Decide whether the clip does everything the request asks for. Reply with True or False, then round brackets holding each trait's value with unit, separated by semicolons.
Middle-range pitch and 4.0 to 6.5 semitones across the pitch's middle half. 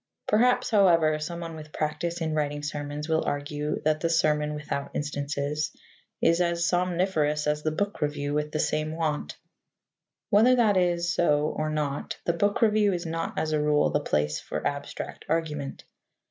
False (155 Hz; 2.5 semitones)